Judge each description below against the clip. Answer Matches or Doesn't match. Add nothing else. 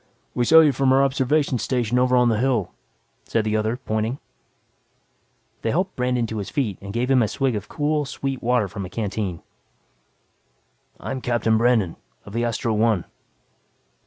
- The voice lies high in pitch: Doesn't match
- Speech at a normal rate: Matches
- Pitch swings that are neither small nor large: Matches